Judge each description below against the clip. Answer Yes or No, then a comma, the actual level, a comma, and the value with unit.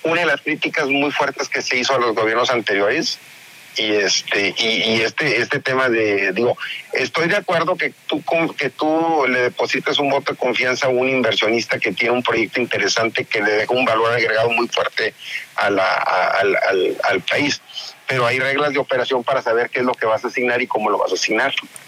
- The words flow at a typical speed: No, fast, 215 wpm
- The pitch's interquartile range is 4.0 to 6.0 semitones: No, average, 2.9 semitones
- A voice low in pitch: Yes, low, 125 Hz